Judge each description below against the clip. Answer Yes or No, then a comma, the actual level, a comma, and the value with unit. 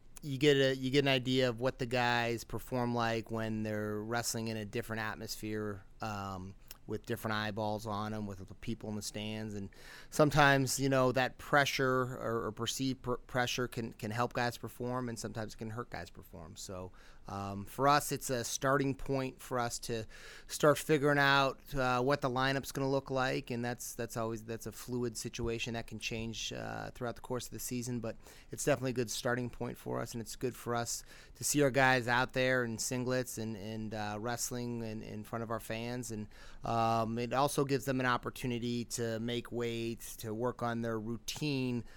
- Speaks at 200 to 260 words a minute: Yes, fast, 205 wpm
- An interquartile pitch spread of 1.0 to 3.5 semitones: Yes, narrow, 2.5 semitones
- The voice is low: Yes, low, 120 Hz